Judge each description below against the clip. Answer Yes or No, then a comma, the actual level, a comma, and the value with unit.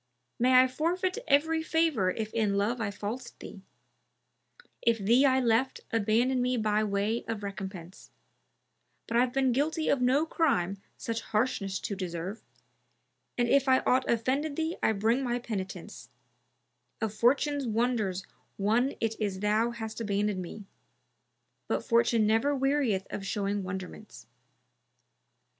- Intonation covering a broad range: No, average, 4.2 semitones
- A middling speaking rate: Yes, average, 145 wpm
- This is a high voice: Yes, high, 230 Hz